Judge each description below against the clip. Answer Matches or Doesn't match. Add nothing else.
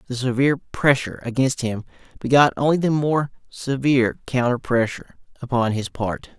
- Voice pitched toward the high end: Doesn't match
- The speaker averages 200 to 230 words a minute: Doesn't match